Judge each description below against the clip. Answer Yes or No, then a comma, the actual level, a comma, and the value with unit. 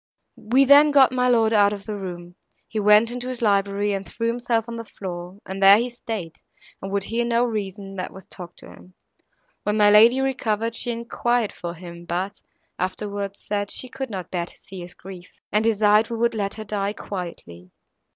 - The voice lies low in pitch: No, high, 210 Hz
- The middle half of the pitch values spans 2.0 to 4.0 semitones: Yes, average, 3.3 semitones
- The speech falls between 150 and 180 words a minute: No, average, 200 wpm